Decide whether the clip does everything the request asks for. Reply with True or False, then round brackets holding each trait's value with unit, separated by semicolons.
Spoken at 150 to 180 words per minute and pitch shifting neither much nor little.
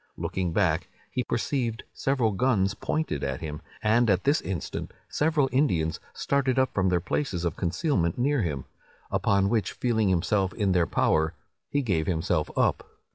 False (160 wpm; 7.1 semitones)